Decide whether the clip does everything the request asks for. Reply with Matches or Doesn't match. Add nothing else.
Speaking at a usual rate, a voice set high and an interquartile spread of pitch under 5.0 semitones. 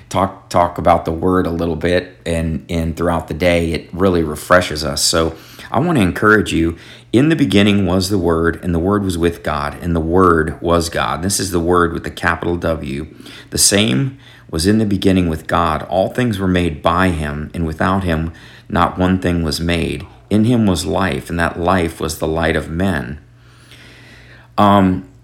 Doesn't match